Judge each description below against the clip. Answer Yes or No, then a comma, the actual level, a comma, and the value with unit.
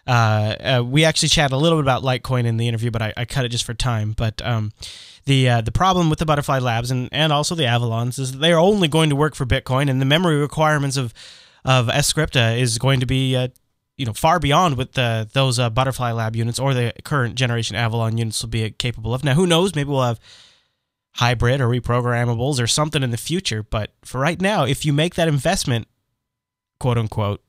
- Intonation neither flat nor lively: Yes, average, 3.7 semitones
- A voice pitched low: Yes, low, 125 Hz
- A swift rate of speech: Yes, fast, 225 wpm